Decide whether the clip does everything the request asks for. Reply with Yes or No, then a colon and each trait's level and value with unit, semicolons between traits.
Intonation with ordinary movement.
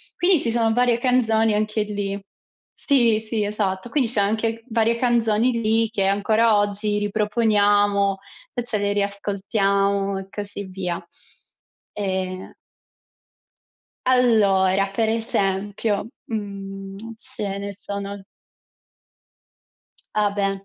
No: narrow, 2.2 semitones